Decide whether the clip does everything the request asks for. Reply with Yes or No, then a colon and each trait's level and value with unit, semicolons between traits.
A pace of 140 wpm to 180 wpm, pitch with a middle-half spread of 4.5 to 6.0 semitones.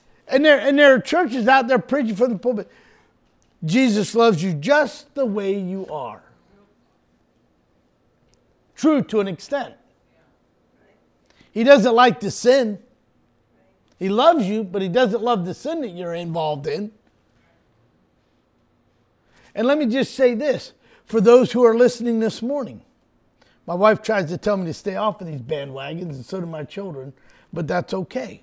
Yes: average, 160 wpm; wide, 5.4 semitones